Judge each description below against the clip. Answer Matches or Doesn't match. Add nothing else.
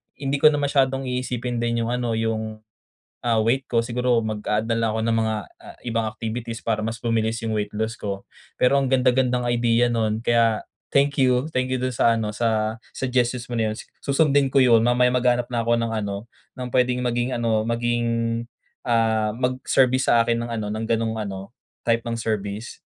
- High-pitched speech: Doesn't match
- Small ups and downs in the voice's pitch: Matches